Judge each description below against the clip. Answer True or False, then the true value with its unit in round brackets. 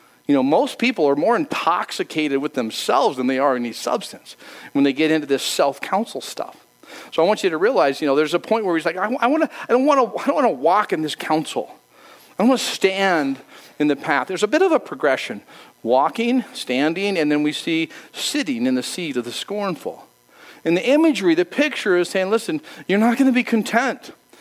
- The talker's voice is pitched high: True (200 Hz)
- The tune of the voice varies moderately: False (8.9 semitones)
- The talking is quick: True (225 wpm)